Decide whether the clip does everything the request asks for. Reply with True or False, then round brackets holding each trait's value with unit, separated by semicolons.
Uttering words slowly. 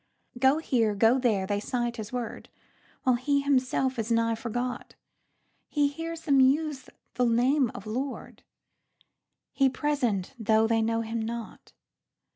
True (125 wpm)